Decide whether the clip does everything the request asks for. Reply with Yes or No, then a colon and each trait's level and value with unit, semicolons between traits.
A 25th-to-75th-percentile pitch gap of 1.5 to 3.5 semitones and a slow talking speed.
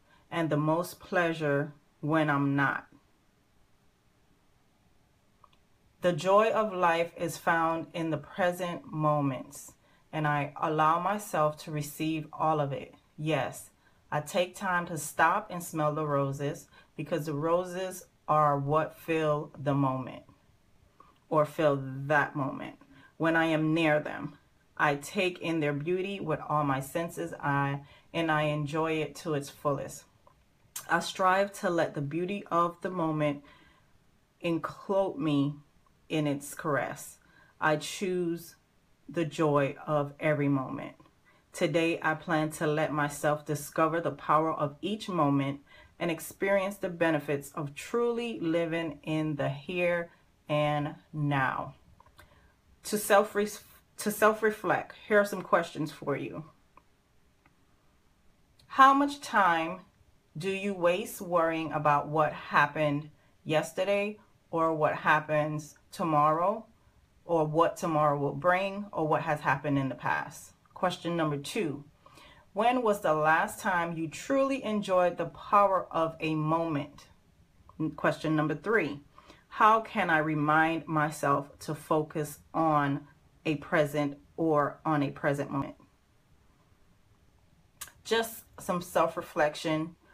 Yes: average, 2.9 semitones; slow, 125 wpm